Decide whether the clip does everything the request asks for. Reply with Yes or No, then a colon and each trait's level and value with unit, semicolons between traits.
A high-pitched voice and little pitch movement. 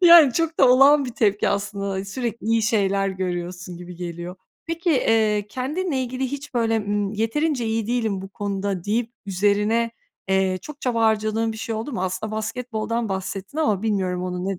No: high, 215 Hz; average, 4.0 semitones